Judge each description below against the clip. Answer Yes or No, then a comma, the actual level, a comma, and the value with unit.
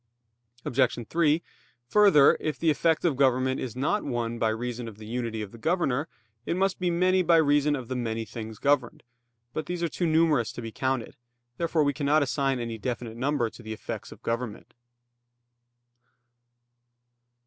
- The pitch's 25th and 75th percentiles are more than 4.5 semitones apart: Yes, average, 5.0 semitones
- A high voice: No, low, 130 Hz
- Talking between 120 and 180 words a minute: Yes, average, 170 wpm